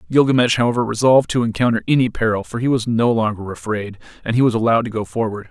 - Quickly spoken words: Yes, fast, 220 wpm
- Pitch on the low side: Yes, low, 115 Hz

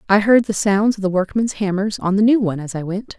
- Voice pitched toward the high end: Yes, high, 200 Hz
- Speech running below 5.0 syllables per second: No, 6.0 syllables/s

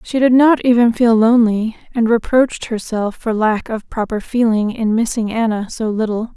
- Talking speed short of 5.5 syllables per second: Yes, 5.0 syllables/s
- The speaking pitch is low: No, high, 225 Hz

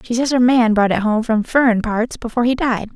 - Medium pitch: No, high, 230 Hz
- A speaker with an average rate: No, fast, 265 wpm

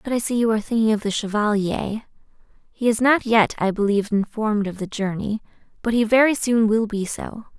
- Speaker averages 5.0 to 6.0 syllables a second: Yes, 5.7 syllables/s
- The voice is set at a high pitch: Yes, high, 220 Hz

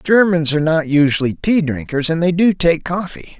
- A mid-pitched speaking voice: Yes, medium, 160 Hz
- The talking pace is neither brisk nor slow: Yes, average, 195 wpm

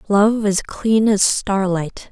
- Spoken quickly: No, average, 140 wpm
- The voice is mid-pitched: No, high, 205 Hz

